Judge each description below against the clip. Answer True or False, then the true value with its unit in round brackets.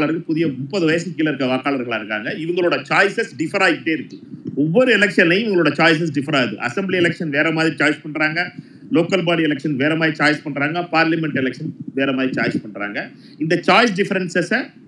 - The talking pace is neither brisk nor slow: False (165 wpm)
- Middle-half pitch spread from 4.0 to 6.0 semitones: False (3.1 semitones)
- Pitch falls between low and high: True (160 Hz)